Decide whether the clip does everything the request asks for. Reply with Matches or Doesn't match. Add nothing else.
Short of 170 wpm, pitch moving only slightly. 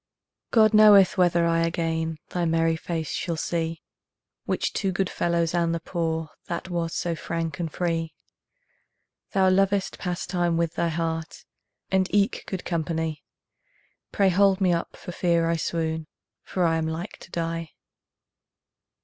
Matches